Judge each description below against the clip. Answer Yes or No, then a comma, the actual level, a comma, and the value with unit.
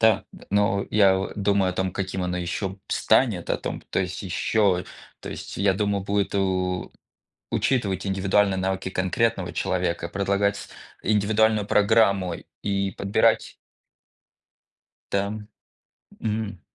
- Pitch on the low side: Yes, low, 100 Hz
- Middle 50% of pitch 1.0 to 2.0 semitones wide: Yes, narrow, 1.5 semitones